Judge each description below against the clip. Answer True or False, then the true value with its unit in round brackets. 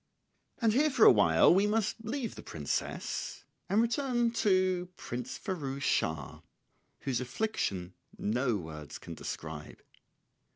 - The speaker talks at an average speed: False (130 wpm)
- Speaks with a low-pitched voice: False (175 Hz)